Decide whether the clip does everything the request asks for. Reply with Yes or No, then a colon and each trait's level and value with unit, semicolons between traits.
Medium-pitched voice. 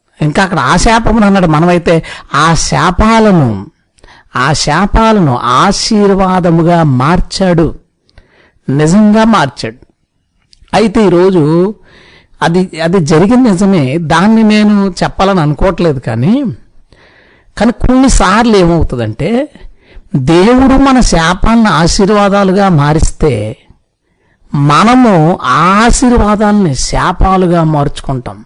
Yes: medium, 180 Hz